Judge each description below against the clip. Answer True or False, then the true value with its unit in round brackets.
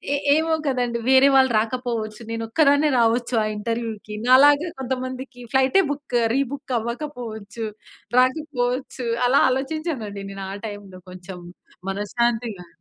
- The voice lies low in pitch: False (245 Hz)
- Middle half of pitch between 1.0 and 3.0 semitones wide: False (3.6 semitones)